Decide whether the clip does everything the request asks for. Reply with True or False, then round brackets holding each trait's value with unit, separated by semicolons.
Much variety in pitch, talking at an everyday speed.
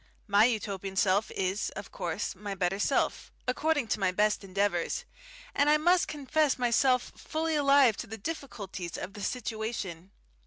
True (6.1 semitones; 155 wpm)